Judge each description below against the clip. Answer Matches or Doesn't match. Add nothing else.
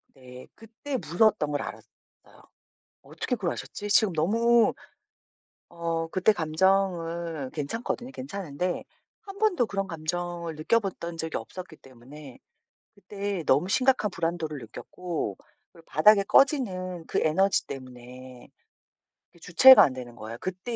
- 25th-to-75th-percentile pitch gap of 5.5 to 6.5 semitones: Doesn't match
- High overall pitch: Doesn't match